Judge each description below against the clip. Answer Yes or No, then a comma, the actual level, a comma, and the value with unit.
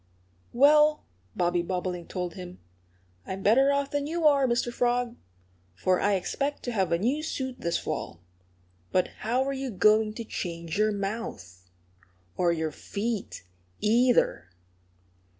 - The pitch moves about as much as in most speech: No, wide, 6.4 semitones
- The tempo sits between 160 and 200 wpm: No, average, 140 wpm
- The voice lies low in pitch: No, high, 215 Hz